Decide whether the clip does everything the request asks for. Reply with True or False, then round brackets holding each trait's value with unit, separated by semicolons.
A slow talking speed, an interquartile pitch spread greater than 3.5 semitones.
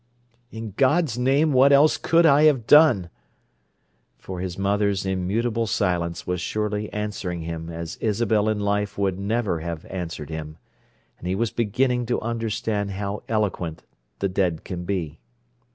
False (150 wpm; 4.4 semitones)